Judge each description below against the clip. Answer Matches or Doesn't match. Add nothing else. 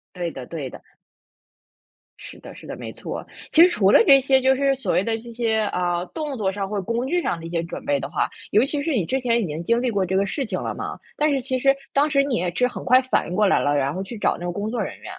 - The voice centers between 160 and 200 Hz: Doesn't match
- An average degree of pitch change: Doesn't match